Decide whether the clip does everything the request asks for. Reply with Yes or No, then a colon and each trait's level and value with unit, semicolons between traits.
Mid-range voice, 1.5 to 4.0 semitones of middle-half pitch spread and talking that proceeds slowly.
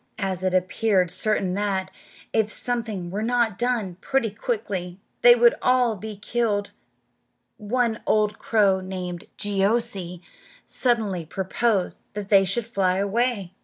No: high, 205 Hz; average, 3.6 semitones; slow, 130 wpm